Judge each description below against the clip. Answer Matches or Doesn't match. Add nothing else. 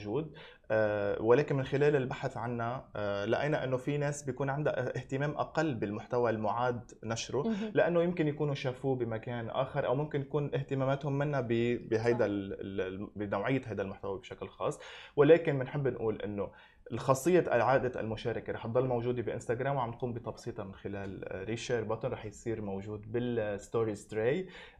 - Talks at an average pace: Doesn't match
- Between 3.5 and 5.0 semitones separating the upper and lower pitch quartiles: Matches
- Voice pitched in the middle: Doesn't match